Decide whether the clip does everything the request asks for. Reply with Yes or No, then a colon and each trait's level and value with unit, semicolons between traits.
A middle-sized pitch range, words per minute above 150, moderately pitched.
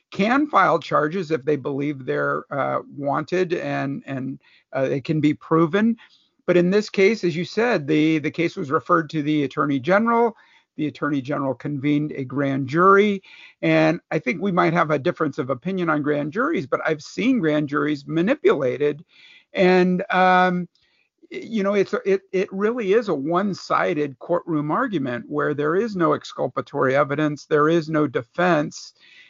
Yes: average, 4.6 semitones; average, 165 wpm; medium, 160 Hz